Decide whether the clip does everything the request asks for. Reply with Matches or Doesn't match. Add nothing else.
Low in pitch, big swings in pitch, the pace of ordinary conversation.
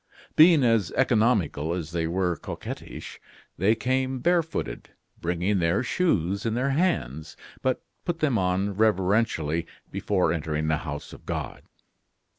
Doesn't match